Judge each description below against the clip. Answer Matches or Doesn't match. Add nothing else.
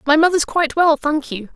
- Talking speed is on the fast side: Matches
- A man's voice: Doesn't match